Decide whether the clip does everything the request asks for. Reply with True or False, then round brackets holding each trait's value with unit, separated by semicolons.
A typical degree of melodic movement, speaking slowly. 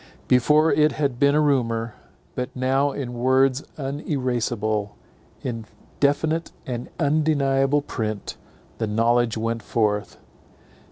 True (3.7 semitones; 110 wpm)